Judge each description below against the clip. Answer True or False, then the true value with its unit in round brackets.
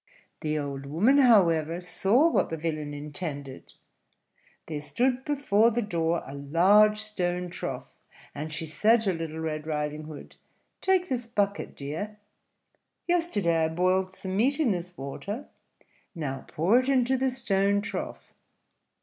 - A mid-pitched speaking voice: True (180 Hz)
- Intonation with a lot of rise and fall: True (6.6 semitones)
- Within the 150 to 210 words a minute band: False (140 wpm)